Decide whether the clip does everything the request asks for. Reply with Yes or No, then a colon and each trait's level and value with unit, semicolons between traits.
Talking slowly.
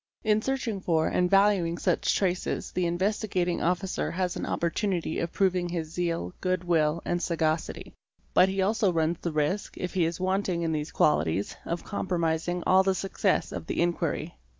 No: average, 175 wpm